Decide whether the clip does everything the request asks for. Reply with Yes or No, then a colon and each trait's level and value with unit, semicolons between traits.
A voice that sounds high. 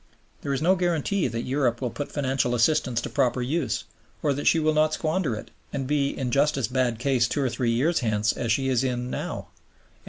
No: low, 135 Hz